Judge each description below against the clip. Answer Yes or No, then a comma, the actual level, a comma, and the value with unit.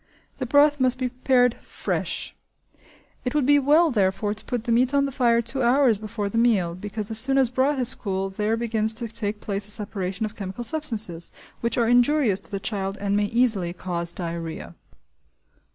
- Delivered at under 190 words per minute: No, average, 195 wpm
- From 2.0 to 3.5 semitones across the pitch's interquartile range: No, average, 4.1 semitones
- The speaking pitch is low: No, high, 225 Hz